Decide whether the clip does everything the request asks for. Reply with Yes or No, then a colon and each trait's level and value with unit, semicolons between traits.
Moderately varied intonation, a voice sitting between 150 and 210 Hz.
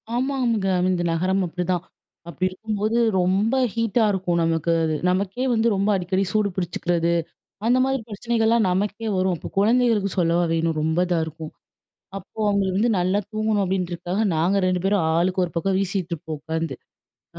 Yes: average, 3.5 semitones; high, 190 Hz